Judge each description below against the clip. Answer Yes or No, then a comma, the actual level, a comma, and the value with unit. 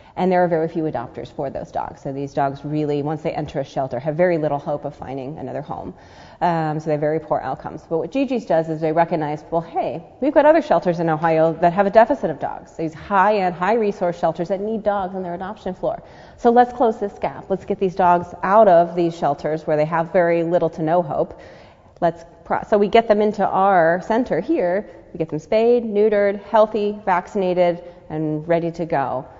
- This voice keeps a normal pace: No, fast, 220 wpm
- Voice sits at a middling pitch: Yes, medium, 175 Hz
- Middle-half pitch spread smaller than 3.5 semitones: No, average, 4.3 semitones